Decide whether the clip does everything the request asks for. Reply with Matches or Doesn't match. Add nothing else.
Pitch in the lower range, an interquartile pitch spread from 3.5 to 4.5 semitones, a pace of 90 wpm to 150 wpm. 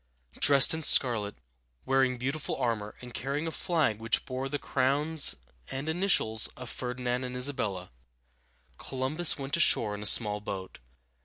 Matches